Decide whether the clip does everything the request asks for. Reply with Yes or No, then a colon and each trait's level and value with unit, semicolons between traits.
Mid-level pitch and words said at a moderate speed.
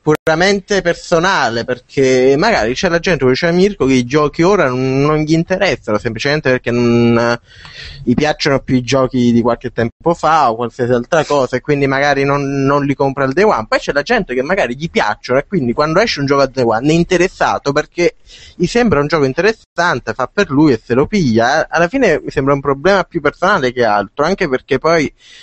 No: medium, 145 Hz; fast, 210 wpm